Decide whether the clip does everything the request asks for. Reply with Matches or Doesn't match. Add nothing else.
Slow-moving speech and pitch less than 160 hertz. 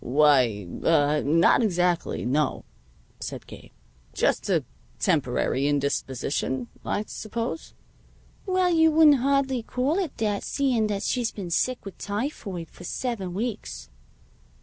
Doesn't match